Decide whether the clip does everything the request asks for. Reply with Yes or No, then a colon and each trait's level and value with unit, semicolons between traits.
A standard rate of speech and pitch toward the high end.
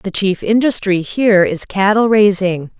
Yes: average, 150 wpm; high, 200 Hz